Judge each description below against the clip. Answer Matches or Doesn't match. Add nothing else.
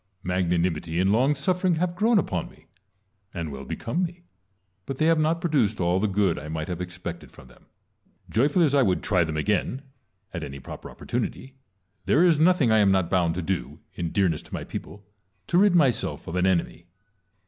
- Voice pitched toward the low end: Matches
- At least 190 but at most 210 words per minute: Matches